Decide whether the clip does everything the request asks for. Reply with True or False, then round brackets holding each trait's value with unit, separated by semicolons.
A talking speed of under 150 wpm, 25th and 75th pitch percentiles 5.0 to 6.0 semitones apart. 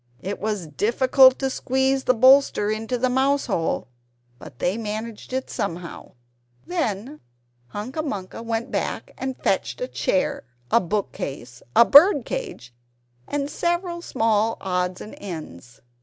True (140 wpm; 5.3 semitones)